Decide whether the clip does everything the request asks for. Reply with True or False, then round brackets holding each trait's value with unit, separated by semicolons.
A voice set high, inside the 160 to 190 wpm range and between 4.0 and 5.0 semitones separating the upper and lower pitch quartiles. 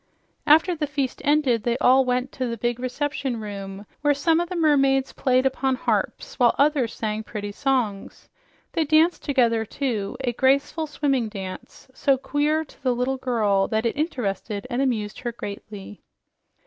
True (255 Hz; 165 wpm; 4.4 semitones)